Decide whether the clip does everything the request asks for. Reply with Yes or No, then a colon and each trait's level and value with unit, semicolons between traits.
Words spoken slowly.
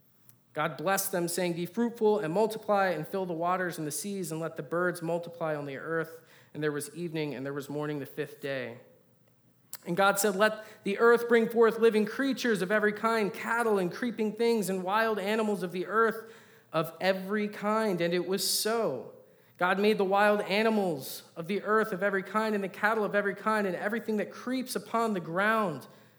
No: average, 200 wpm